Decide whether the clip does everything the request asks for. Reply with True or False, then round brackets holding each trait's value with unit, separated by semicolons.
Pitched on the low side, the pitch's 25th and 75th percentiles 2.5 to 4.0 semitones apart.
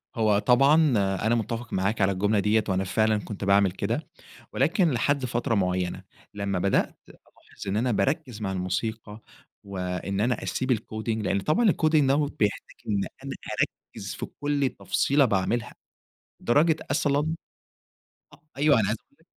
False (110 Hz; 5.3 semitones)